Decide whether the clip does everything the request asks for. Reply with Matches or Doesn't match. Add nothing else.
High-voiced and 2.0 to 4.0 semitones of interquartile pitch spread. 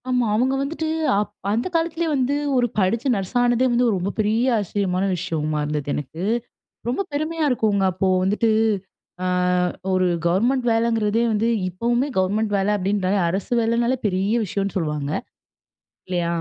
Doesn't match